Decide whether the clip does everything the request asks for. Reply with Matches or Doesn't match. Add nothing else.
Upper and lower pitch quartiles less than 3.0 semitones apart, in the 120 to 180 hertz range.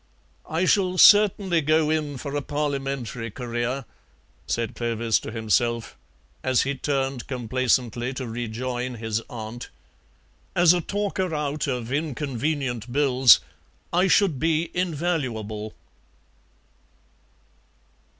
Doesn't match